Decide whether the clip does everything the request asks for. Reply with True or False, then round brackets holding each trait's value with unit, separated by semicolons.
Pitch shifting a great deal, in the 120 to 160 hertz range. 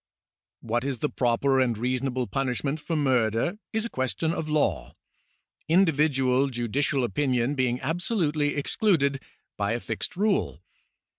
False (3.7 semitones; 135 Hz)